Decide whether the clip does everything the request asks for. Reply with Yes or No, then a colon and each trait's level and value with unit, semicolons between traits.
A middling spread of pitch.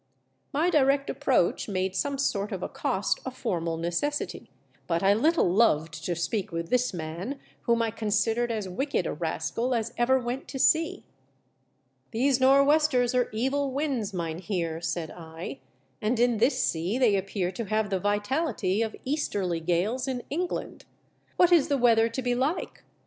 No: wide, 6.7 semitones